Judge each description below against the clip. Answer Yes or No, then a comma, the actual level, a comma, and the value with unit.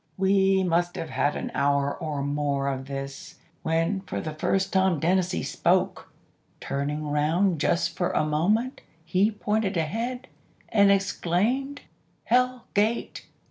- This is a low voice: No, medium, 175 Hz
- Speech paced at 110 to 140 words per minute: Yes, slow, 135 wpm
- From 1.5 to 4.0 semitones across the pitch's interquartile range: No, average, 5.2 semitones